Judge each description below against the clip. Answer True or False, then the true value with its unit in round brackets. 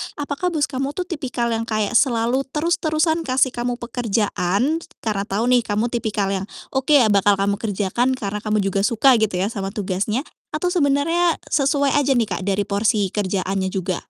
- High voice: True (230 Hz)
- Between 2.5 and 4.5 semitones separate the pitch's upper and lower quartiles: False (5.4 semitones)